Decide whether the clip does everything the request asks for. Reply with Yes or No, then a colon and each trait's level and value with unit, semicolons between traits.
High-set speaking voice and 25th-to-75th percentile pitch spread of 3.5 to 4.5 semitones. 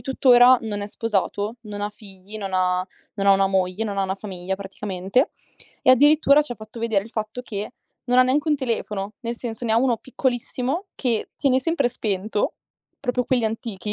Yes: high, 220 Hz; average, 4.0 semitones